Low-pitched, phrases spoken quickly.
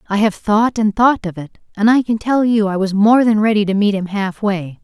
No: high, 210 Hz; fast, 260 wpm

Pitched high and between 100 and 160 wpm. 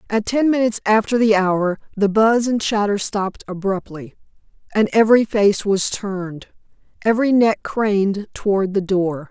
Yes: high, 205 Hz; average, 150 wpm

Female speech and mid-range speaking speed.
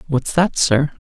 No: male; average, 170 wpm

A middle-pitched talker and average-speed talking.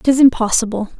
No: high, 235 Hz; average, 180 wpm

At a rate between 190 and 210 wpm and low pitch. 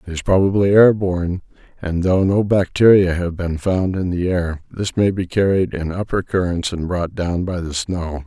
Yes: fast, 205 wpm; very low, 90 Hz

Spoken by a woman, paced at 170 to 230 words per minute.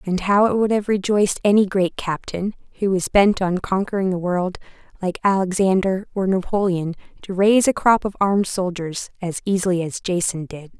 Yes: female; average, 180 wpm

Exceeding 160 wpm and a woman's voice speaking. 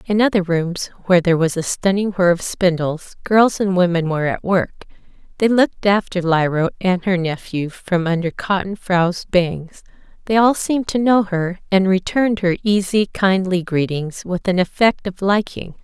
Yes: average, 175 wpm; female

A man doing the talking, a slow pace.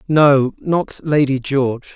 Yes: male; slow, 90 wpm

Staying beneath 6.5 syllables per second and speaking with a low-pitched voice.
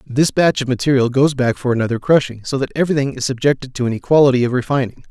No: 6.9 syllables/s; low, 130 Hz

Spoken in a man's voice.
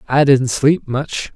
Yes: male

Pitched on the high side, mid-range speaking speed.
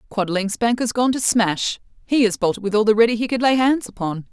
No: high, 225 Hz; fast, 250 wpm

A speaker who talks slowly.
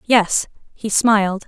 Yes: slow, 120 wpm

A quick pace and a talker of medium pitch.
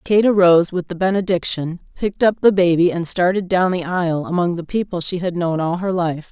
Yes: fast, 220 wpm; medium, 180 Hz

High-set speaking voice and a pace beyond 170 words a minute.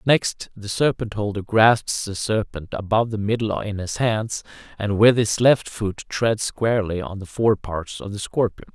No: low, 105 Hz; average, 180 wpm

